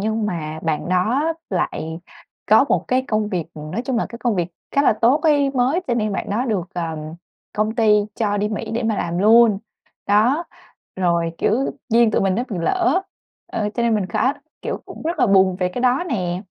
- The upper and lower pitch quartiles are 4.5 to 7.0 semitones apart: Yes, average, 5.2 semitones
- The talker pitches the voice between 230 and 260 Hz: No, high, 215 Hz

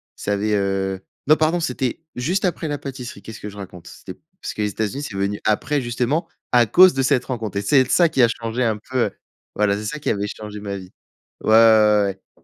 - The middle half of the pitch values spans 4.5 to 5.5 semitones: Yes, average, 5.2 semitones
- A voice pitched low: Yes, low, 115 Hz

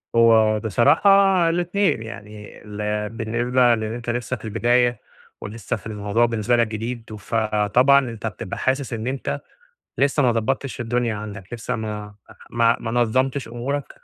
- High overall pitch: No, low, 115 Hz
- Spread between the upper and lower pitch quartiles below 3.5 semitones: Yes, narrow, 2.6 semitones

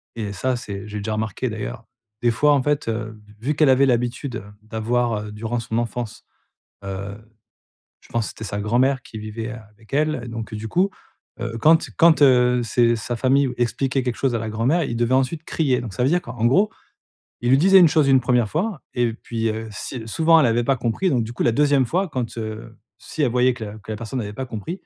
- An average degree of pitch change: Yes, average, 3.5 semitones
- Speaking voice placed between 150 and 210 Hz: No, low, 120 Hz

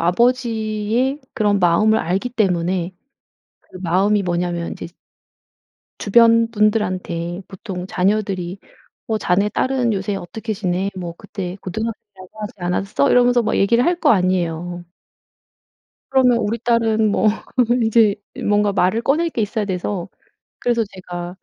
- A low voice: No, high, 205 Hz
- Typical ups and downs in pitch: Yes, average, 4.0 semitones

